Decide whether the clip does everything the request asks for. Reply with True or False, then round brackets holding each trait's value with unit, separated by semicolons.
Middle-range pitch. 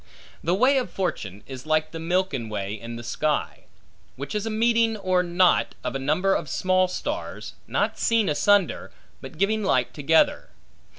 True (180 Hz)